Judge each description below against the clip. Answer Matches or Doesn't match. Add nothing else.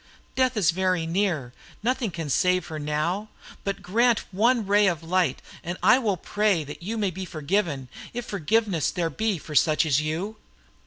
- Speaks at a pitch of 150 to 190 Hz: Matches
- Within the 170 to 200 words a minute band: Matches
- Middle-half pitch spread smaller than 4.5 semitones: Doesn't match